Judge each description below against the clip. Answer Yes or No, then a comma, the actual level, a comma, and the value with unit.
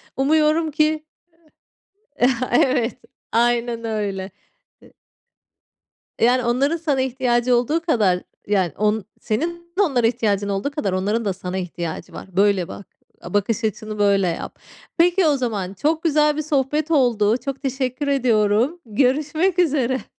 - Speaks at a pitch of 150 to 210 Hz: No, high, 245 Hz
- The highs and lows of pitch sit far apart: Yes, wide, 6.3 semitones